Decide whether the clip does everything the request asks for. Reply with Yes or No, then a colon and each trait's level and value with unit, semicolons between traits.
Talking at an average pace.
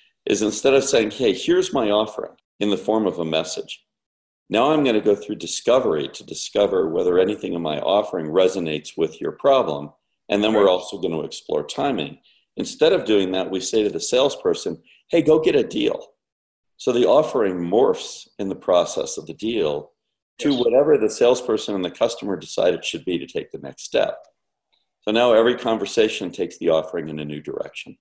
Yes: average, 195 wpm